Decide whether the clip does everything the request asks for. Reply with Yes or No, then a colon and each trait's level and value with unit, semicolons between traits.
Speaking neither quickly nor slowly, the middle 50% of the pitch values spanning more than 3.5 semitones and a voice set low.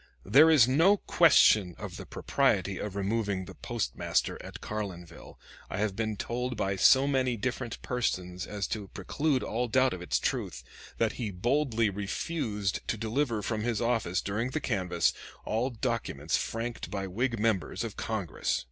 Yes: average, 160 wpm; average, 4.1 semitones; low, 110 Hz